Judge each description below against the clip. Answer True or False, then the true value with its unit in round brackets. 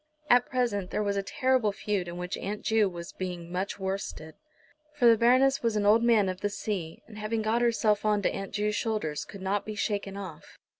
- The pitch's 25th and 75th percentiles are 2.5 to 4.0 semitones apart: True (2.8 semitones)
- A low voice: False (205 Hz)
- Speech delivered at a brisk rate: True (215 wpm)